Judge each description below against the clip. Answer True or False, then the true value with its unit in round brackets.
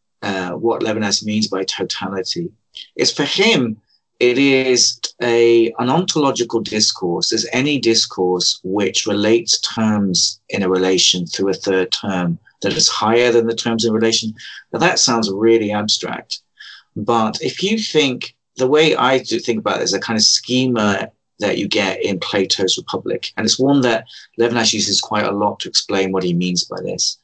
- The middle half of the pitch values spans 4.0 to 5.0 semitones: False (3.0 semitones)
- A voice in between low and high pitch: False (115 Hz)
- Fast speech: False (175 wpm)